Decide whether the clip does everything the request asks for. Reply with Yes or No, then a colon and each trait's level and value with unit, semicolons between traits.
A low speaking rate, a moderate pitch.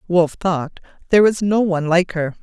No: average, 200 wpm; medium, 175 Hz